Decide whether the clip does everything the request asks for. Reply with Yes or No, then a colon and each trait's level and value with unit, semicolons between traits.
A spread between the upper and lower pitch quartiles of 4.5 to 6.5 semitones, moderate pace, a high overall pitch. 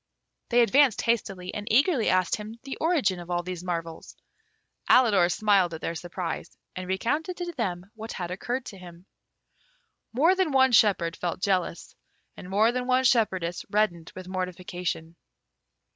Yes: wide, 5.4 semitones; average, 155 wpm; high, 195 Hz